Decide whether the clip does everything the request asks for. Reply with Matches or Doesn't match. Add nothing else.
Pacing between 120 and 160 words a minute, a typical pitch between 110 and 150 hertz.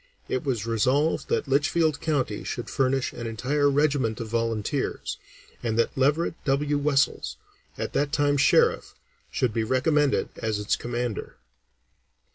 Matches